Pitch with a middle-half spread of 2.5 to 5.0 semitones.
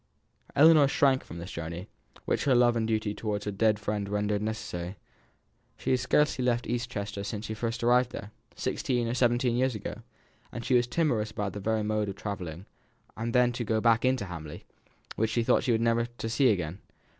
Yes: average, 2.9 semitones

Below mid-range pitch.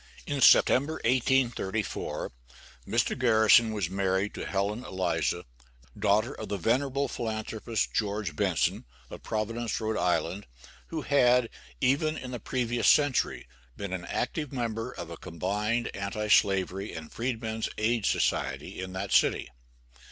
Yes: low, 110 Hz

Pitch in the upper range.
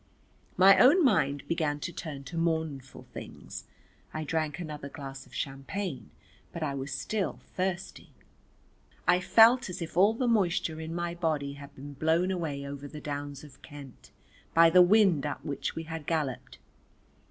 No: medium, 160 Hz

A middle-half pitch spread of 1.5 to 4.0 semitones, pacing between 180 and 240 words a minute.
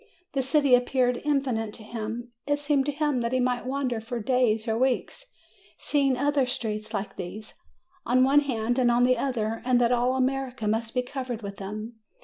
Yes: average, 3.0 semitones; average, 190 wpm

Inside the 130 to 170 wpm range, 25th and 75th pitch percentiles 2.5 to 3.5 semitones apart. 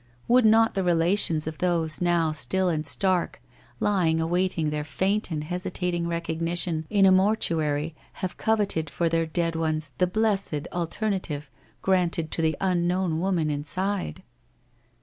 Yes: average, 140 wpm; average, 2.9 semitones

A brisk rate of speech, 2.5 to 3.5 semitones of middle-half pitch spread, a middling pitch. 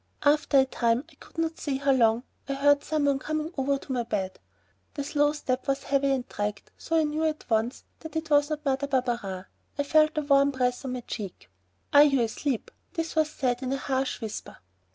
No: fast, 215 wpm; average, 3.2 semitones; very high, 275 Hz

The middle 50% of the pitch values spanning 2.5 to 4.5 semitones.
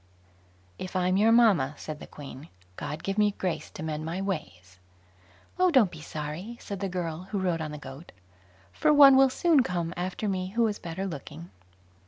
No: average, 5.1 semitones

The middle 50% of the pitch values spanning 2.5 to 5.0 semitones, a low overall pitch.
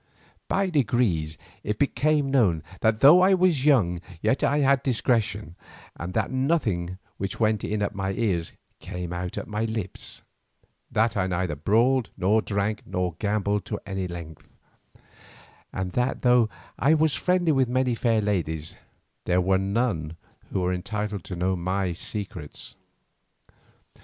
No: wide, 5.6 semitones; low, 105 Hz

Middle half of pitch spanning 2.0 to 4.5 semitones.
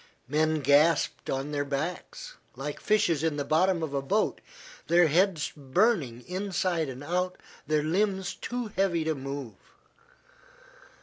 Yes: average, 4.2 semitones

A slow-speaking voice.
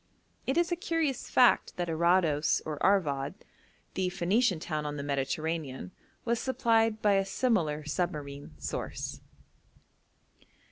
Yes: slow, 125 wpm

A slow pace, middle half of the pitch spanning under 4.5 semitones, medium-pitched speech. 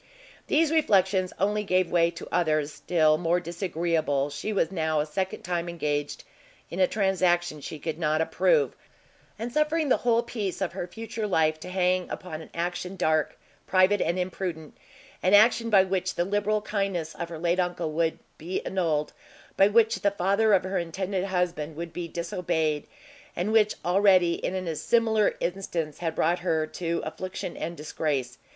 No: average, 170 wpm; average, 3.3 semitones; medium, 180 Hz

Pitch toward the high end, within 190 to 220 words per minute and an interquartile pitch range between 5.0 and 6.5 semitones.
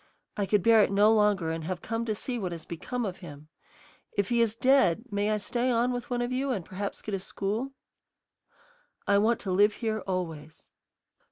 No: high, 210 Hz; fast, 205 wpm; average, 4.1 semitones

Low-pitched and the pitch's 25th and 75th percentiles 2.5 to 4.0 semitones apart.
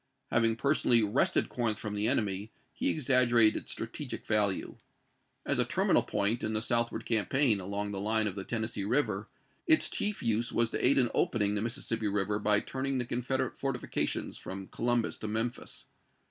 Yes: low, 110 Hz; average, 2.8 semitones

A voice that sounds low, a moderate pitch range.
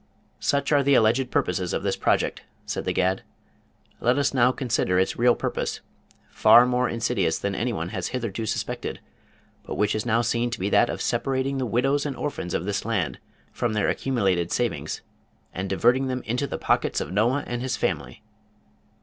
Yes: low, 120 Hz; average, 4.4 semitones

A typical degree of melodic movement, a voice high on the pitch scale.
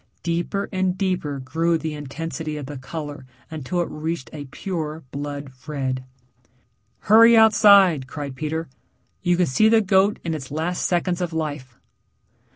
No: average, 4.0 semitones; medium, 160 Hz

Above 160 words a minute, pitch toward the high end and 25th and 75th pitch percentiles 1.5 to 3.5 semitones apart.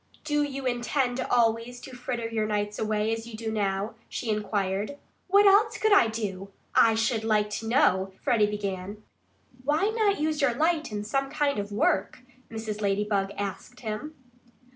No: average, 170 wpm; high, 225 Hz; average, 4.5 semitones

